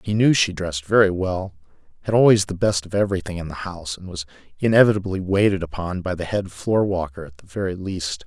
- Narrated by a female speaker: No, male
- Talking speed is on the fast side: Yes, fast, 210 wpm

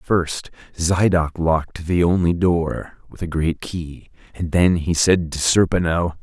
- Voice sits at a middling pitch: No, very low, 85 Hz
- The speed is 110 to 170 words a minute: Yes, average, 155 wpm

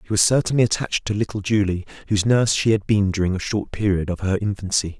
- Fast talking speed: Yes, fast, 230 wpm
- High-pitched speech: No, low, 100 Hz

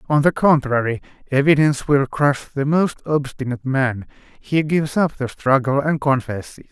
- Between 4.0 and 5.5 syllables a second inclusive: Yes, 5.0 syllables/s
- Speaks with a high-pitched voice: No, medium, 140 Hz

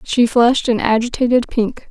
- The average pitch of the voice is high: Yes, high, 235 Hz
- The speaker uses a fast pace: No, average, 160 wpm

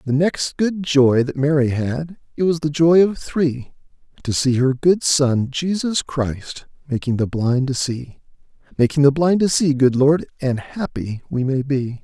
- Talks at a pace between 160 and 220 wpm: Yes, average, 185 wpm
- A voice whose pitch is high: No, medium, 140 Hz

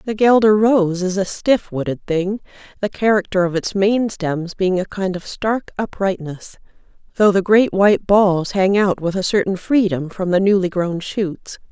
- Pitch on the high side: Yes, high, 195 Hz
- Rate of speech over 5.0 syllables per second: No, 4.4 syllables/s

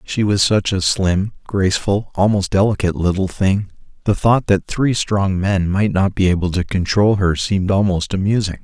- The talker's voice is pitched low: Yes, very low, 95 Hz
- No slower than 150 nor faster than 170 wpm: No, average, 180 wpm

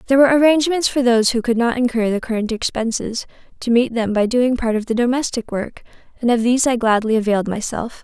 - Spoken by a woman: Yes, female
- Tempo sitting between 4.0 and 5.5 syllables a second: No, 6.5 syllables/s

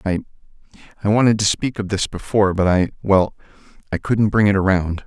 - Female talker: No, male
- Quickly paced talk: No, average, 165 wpm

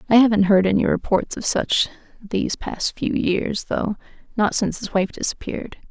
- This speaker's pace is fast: No, average, 165 wpm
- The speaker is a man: No, female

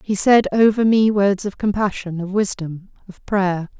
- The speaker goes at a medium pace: Yes, average, 175 wpm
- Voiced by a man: No, female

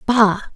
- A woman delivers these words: Yes, female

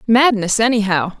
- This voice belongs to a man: No, female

